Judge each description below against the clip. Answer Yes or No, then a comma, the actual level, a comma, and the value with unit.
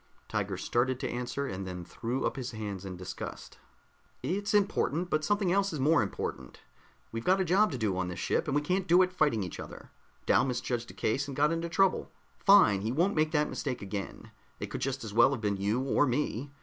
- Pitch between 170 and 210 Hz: No, low, 135 Hz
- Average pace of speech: No, fast, 225 wpm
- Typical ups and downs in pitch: No, wide, 7.3 semitones